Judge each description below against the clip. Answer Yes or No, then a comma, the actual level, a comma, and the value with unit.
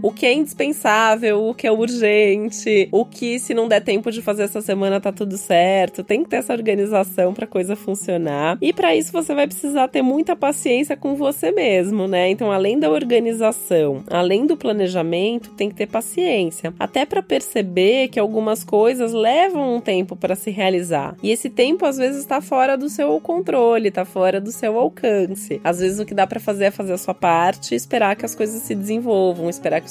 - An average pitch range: Yes, average, 4.3 semitones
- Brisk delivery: Yes, fast, 205 wpm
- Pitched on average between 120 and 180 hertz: No, high, 210 Hz